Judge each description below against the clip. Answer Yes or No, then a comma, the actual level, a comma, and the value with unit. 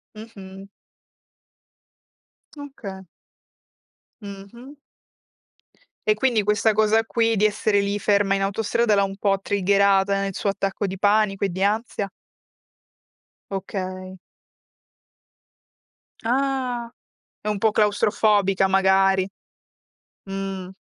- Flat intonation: Yes, narrow, 1.9 semitones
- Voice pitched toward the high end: Yes, high, 200 Hz